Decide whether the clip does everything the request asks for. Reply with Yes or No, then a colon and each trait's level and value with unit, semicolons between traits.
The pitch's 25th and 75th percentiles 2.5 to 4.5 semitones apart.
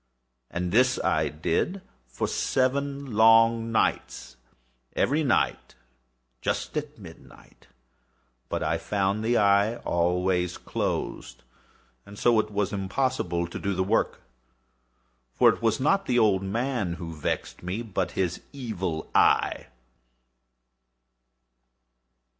No: average, 5.3 semitones